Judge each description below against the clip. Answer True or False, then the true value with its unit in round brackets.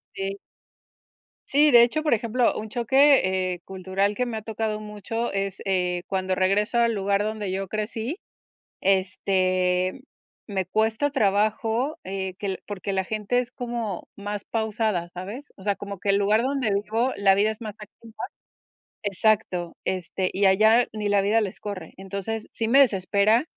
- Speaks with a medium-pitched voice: False (205 Hz)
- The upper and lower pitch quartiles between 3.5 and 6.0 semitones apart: False (2.8 semitones)